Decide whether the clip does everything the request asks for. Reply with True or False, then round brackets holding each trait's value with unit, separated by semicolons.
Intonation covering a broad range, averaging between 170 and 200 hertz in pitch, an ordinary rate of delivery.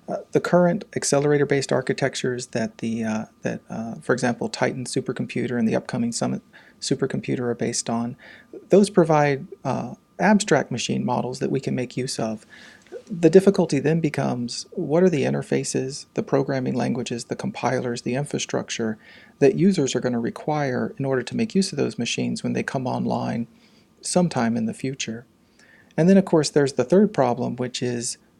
False (6.8 semitones; 135 Hz; 175 wpm)